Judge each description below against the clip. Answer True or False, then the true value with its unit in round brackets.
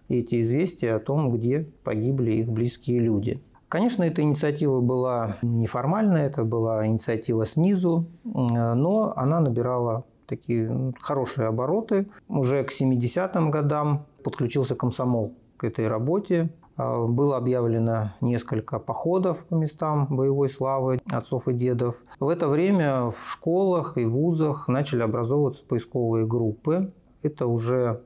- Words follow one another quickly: False (120 wpm)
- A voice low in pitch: True (130 Hz)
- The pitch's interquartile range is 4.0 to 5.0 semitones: True (4.4 semitones)